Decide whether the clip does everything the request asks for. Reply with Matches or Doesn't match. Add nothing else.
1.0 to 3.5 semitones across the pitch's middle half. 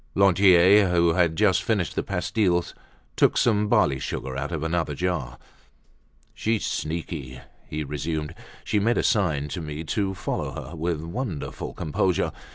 Doesn't match